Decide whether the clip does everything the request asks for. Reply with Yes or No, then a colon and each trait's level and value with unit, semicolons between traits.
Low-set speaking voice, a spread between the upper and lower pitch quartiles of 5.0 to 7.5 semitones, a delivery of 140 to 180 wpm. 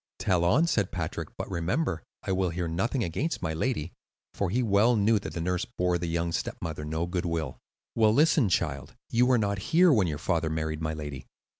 No: very low, 90 Hz; wide, 5.4 semitones; fast, 205 wpm